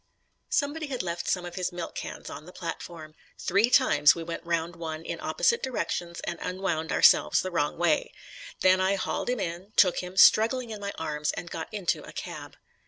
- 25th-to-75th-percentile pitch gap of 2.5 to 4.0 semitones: Yes, average, 3.1 semitones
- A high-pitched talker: No, medium, 175 Hz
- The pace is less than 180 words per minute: No, average, 195 wpm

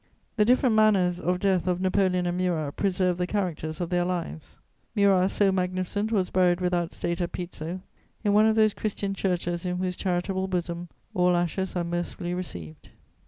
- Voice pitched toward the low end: No, medium, 180 Hz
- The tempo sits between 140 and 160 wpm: No, average, 175 wpm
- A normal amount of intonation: No, narrow, 1.8 semitones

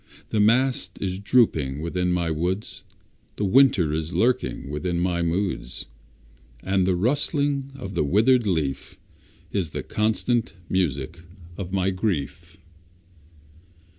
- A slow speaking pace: Yes, slow, 120 wpm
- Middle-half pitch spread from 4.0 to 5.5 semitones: Yes, average, 4.7 semitones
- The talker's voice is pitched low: Yes, very low, 95 Hz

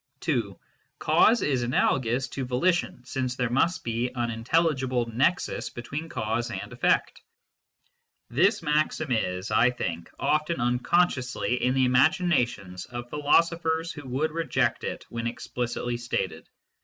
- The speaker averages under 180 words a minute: Yes, slow, 135 wpm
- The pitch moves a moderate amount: Yes, average, 4.3 semitones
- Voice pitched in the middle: No, low, 125 Hz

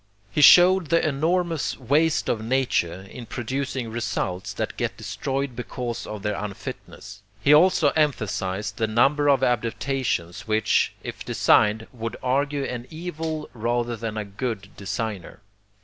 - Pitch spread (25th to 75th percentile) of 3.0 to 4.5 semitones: No, average, 4.9 semitones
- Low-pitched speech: Yes, low, 120 Hz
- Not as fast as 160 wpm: Yes, slow, 135 wpm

